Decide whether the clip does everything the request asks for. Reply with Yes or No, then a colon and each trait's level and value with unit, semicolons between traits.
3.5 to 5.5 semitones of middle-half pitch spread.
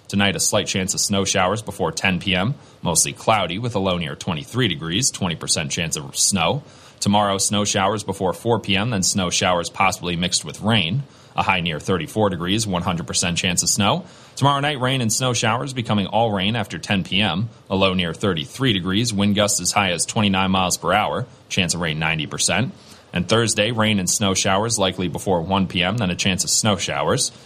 No: average, 2.9 semitones